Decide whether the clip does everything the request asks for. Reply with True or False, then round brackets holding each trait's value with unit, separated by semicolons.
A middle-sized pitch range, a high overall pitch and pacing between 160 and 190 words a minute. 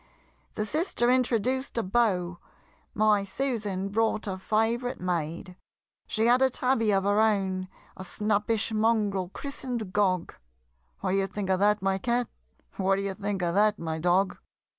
False (3.2 semitones; 205 Hz; 150 wpm)